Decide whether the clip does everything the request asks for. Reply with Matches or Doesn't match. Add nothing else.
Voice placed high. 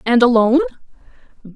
Matches